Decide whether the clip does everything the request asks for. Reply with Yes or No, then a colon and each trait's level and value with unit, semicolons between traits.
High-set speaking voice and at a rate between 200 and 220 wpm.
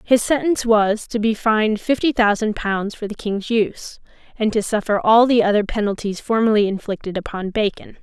No: high, 215 Hz; average, 180 wpm